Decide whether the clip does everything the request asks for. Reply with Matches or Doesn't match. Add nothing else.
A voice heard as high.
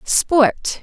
Matches